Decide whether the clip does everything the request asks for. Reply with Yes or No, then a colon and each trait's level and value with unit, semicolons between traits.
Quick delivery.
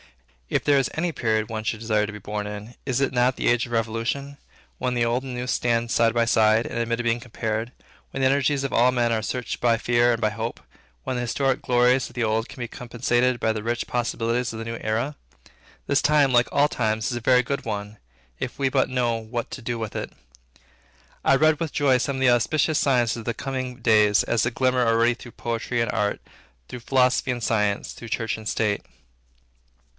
Yes: fast, 225 wpm